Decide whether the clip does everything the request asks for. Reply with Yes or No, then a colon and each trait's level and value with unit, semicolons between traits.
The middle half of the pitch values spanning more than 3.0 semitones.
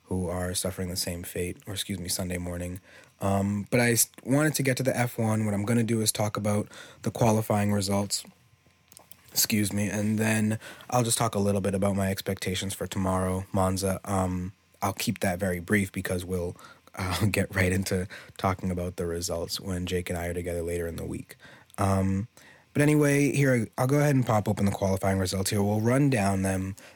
No: average, 2.7 semitones